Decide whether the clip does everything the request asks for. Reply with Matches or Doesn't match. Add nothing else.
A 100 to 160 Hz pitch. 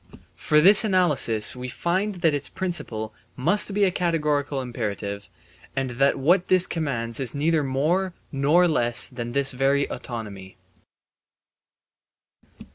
Matches